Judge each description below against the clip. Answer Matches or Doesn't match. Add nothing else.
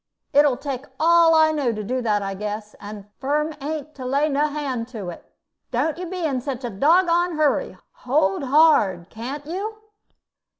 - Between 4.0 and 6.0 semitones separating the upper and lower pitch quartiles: Matches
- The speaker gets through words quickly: Doesn't match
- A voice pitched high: Matches